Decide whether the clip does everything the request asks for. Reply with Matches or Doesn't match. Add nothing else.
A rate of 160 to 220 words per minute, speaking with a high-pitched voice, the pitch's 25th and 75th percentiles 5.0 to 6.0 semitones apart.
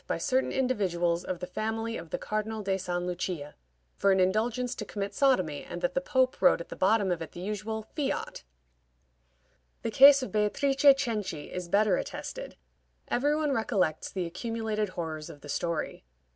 Matches